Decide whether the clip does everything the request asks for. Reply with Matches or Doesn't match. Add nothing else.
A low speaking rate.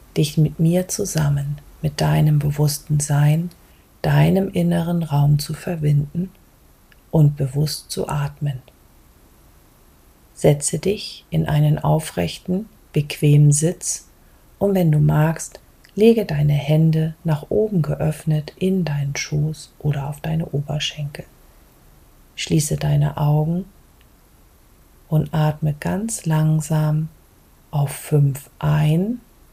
Matches